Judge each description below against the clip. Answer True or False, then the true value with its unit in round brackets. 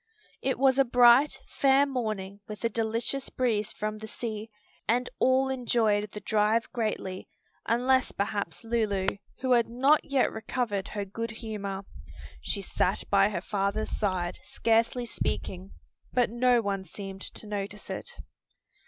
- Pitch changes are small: False (3.4 semitones)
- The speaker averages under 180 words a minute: True (145 wpm)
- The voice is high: True (220 Hz)